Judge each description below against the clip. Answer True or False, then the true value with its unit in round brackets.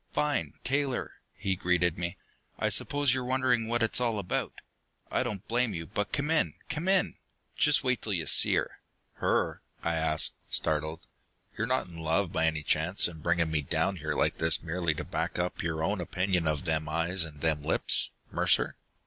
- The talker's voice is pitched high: False (90 Hz)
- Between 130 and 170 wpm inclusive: False (190 wpm)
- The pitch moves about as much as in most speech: False (6.7 semitones)